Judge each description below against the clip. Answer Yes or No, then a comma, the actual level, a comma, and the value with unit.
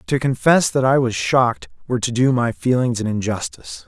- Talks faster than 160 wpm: Yes, average, 200 wpm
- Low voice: Yes, low, 120 Hz